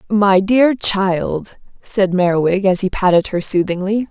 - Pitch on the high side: Yes, high, 195 Hz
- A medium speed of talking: Yes, average, 145 wpm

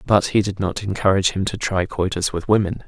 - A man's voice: Yes, male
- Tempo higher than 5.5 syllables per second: Yes, 5.9 syllables/s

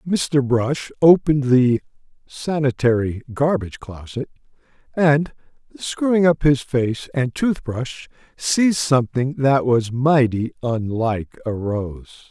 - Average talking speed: No, slow, 110 wpm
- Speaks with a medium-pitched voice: No, low, 130 Hz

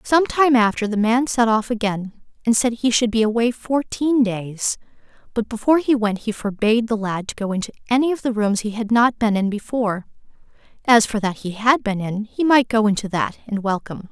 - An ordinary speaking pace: No, fast, 215 wpm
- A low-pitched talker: No, high, 225 Hz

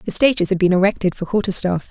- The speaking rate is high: Yes, fast, 250 wpm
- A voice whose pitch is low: No, high, 190 Hz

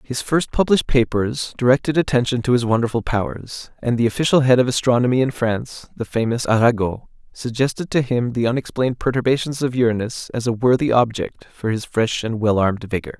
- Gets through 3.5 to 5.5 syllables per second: No, 5.9 syllables/s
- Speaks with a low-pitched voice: Yes, low, 120 Hz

